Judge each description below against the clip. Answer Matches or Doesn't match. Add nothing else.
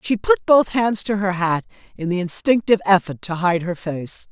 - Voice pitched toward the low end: Doesn't match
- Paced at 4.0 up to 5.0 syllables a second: Matches